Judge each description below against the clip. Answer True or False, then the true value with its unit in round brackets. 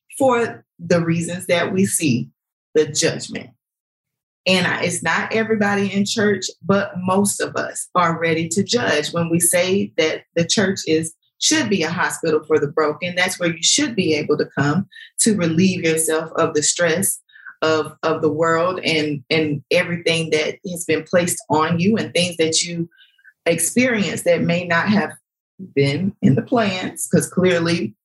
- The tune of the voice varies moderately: True (3.7 semitones)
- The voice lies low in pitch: False (170 Hz)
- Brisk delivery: False (170 wpm)